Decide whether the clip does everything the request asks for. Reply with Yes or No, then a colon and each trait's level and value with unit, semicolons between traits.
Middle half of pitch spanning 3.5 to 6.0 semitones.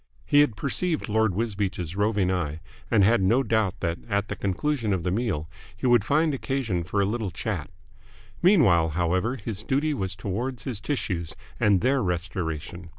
Yes: average, 5.2 semitones